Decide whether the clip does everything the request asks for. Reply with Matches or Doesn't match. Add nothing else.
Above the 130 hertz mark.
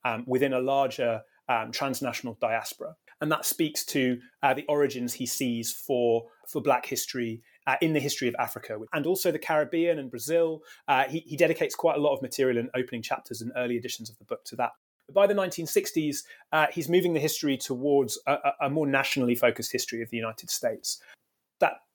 Matches